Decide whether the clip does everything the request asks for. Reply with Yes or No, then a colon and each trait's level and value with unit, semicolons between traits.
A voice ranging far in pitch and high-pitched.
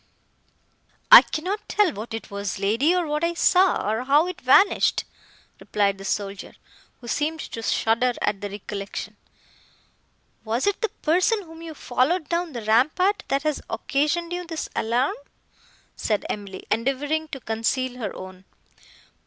Yes: wide, 7.3 semitones; very high, 270 Hz